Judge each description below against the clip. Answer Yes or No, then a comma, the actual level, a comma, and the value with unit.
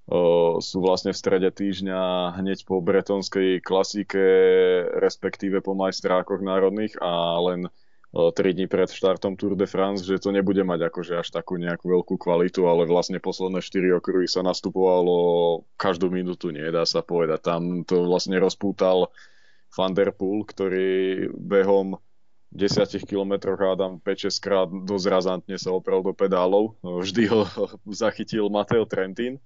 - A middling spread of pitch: No, narrow, 1.6 semitones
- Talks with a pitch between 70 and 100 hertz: Yes, very low, 95 Hz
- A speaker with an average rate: Yes, average, 145 wpm